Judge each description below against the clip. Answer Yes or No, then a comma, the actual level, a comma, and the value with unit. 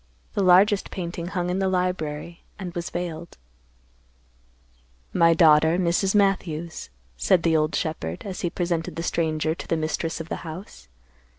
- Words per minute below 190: Yes, average, 155 wpm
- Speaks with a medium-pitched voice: Yes, medium, 170 Hz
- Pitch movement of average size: No, narrow, 2.3 semitones